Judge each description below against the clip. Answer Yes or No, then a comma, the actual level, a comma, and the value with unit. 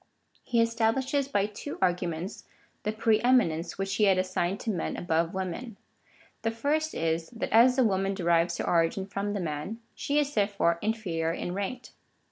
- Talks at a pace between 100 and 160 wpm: No, average, 170 wpm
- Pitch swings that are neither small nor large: Yes, average, 4.9 semitones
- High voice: Yes, high, 200 Hz